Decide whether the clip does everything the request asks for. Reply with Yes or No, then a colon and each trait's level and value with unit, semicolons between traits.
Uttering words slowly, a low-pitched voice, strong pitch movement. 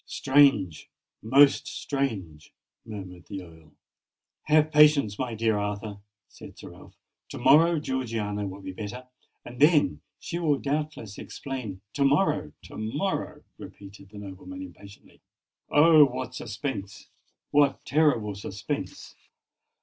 Yes: slow, 110 wpm; low, 120 Hz; wide, 6.4 semitones